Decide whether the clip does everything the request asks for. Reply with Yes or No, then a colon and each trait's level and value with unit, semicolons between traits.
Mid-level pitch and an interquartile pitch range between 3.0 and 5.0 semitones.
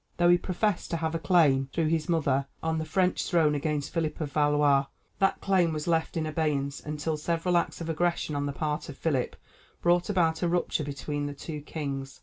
No: medium, 155 Hz; narrow, 2.6 semitones